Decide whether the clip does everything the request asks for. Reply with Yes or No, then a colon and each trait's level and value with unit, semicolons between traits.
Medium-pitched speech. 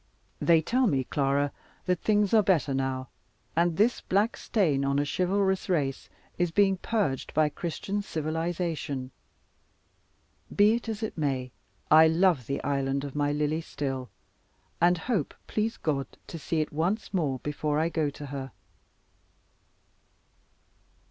Yes: medium, 160 Hz